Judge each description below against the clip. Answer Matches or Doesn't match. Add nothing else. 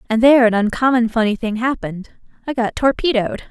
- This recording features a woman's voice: Matches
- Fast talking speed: Doesn't match